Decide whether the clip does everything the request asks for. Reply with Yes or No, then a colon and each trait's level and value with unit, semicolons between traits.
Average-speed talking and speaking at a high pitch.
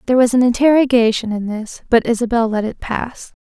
Yes: average, 190 wpm; high, 235 Hz